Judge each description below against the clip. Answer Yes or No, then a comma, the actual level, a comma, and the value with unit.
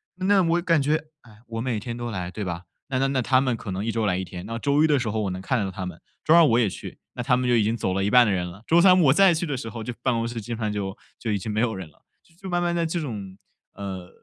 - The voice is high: No, low, 115 Hz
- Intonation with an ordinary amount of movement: No, wide, 5.7 semitones